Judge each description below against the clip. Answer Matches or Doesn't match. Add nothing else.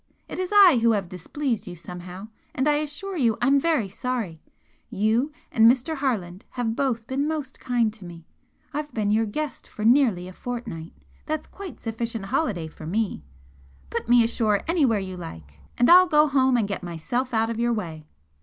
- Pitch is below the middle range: Doesn't match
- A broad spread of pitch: Matches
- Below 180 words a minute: Doesn't match